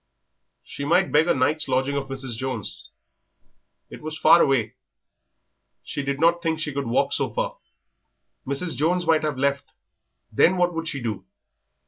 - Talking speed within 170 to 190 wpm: No, average, 160 wpm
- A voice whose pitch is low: No, medium, 145 Hz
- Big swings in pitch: No, average, 3.6 semitones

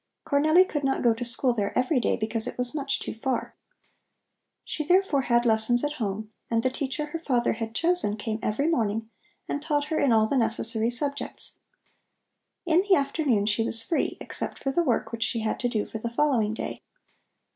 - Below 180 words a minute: No, average, 200 wpm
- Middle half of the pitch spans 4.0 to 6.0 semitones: Yes, average, 4.5 semitones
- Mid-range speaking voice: No, high, 245 Hz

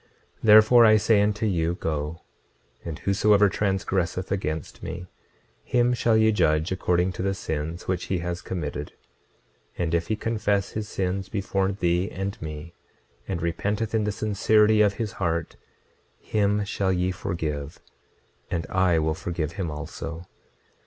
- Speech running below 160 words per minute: Yes, average, 150 wpm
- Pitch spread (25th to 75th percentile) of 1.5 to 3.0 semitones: No, average, 3.7 semitones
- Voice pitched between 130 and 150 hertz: No, very low, 95 Hz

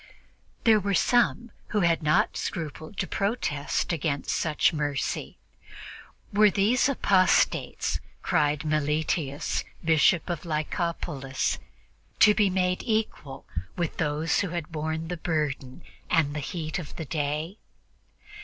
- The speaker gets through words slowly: Yes, slow, 120 wpm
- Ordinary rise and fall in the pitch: Yes, average, 3.7 semitones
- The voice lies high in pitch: No, medium, 160 Hz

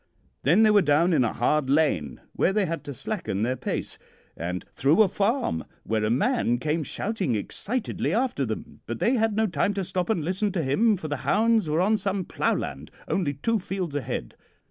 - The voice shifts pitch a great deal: Yes, wide, 7.5 semitones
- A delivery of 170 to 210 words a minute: Yes, average, 200 wpm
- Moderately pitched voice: Yes, medium, 170 Hz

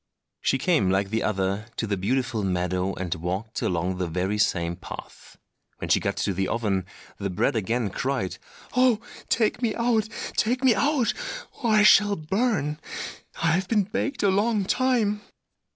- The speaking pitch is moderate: No, low, 125 Hz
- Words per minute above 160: Yes, average, 170 wpm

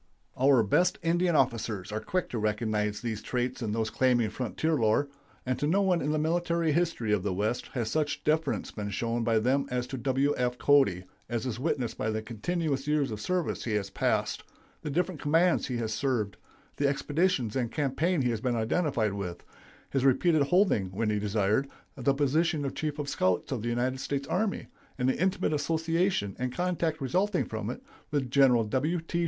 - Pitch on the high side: No, low, 130 Hz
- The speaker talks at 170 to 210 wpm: Yes, average, 195 wpm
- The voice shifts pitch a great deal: Yes, wide, 5.9 semitones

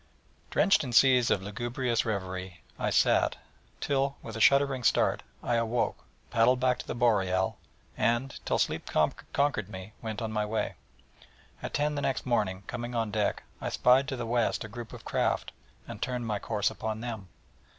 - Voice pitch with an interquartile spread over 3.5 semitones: No, average, 3.1 semitones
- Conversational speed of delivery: Yes, average, 175 wpm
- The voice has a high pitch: No, low, 115 Hz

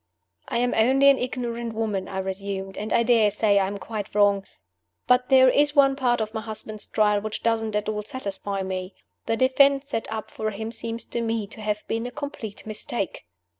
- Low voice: No, high, 220 Hz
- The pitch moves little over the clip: No, average, 3.0 semitones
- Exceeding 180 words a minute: Yes, fast, 205 wpm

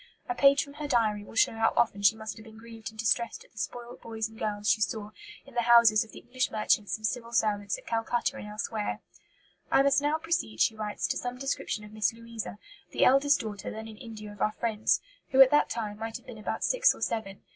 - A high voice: Yes, high, 225 Hz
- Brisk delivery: Yes, fast, 240 wpm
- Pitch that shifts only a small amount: Yes, narrow, 2.3 semitones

